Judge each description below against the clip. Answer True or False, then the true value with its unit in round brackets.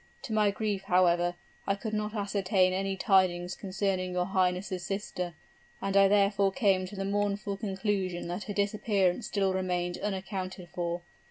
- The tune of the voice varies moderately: False (1.7 semitones)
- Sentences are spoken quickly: False (155 wpm)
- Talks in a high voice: True (195 Hz)